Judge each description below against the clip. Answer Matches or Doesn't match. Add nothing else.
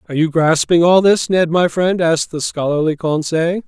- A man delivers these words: Matches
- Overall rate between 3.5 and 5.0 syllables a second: Doesn't match